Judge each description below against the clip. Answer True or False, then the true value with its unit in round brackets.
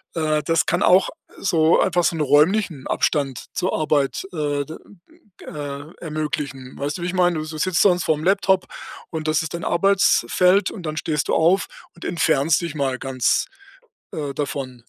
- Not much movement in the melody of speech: False (3.4 semitones)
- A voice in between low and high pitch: True (155 Hz)